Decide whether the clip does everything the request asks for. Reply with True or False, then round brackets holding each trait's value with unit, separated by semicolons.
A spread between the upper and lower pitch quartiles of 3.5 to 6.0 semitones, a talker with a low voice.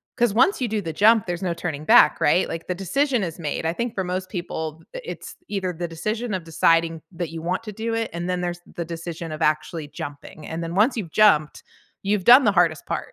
False (4.3 semitones; 175 Hz)